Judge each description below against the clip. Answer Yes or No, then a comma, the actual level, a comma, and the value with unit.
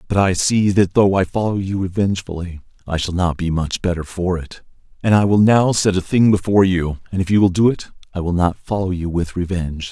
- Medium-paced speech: No, fast, 235 wpm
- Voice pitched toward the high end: No, very low, 95 Hz